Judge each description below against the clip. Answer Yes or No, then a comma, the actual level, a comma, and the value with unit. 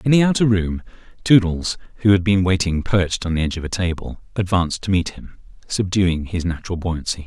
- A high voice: No, very low, 95 Hz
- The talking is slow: No, average, 200 wpm